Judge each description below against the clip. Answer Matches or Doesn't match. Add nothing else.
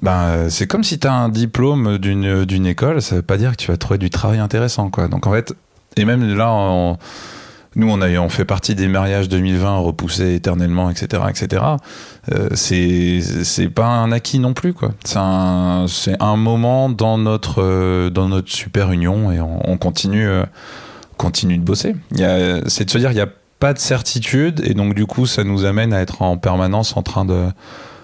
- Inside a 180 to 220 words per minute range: Matches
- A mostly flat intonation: Doesn't match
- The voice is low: Matches